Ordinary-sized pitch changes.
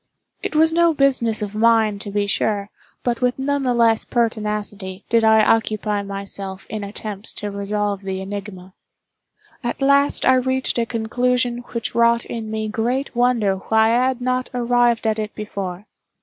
Yes: average, 3.1 semitones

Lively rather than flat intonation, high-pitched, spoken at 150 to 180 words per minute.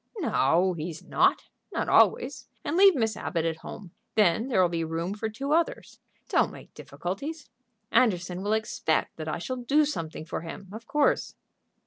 Yes: wide, 7.4 semitones; high, 200 Hz; average, 165 wpm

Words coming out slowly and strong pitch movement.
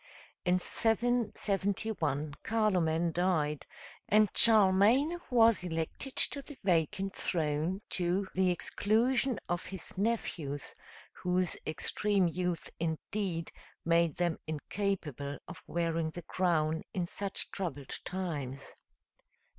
No: slow, 100 wpm; average, 4.0 semitones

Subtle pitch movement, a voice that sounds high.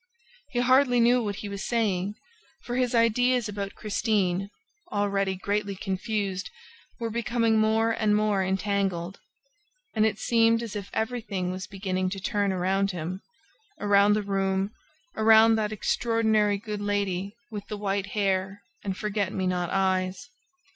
Yes: narrow, 2.3 semitones; high, 205 Hz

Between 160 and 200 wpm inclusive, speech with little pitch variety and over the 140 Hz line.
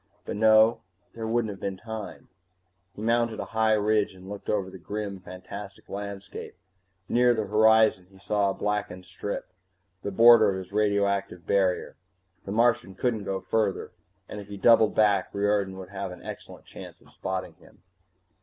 No: average, 170 wpm; narrow, 2.2 semitones; low, 100 Hz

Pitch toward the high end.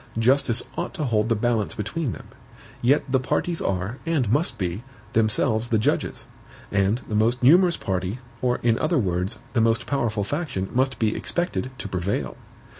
No: low, 115 Hz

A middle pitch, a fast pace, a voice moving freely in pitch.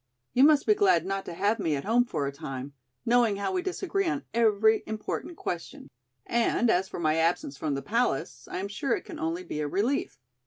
No: high, 200 Hz; fast, 220 wpm; wide, 6.5 semitones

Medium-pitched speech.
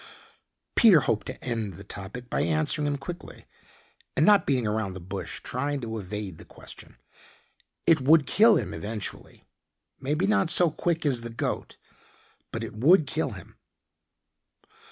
No: low, 125 Hz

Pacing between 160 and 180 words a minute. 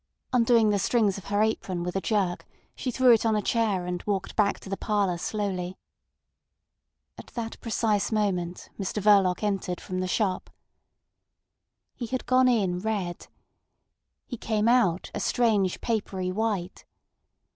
No: average, 150 wpm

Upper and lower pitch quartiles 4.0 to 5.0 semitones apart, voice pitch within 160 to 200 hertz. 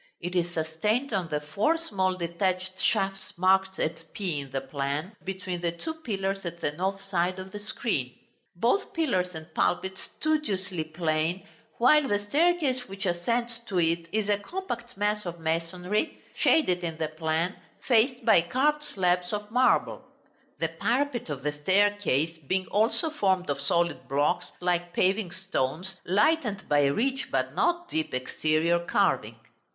Yes: average, 4.5 semitones; medium, 185 Hz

